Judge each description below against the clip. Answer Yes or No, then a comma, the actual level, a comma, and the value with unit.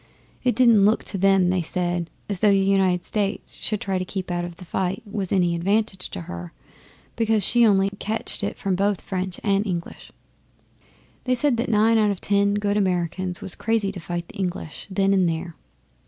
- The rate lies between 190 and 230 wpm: Yes, average, 195 wpm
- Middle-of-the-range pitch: No, high, 195 Hz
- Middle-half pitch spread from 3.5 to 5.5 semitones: No, narrow, 2.6 semitones